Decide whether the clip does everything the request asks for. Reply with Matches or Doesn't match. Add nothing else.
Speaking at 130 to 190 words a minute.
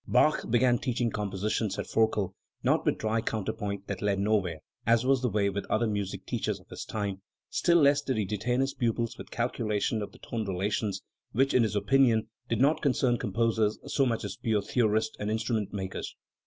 Doesn't match